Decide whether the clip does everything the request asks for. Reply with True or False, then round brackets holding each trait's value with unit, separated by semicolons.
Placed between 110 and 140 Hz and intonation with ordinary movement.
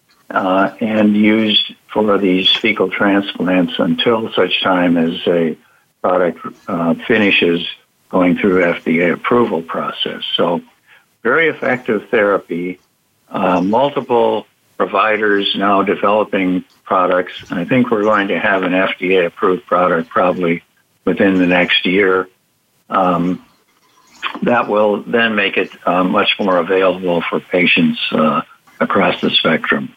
False (95 Hz; 3.0 semitones)